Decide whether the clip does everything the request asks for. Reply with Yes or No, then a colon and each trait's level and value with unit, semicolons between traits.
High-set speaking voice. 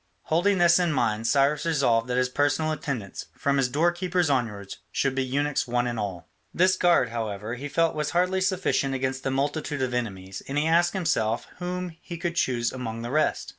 No: medium, 140 Hz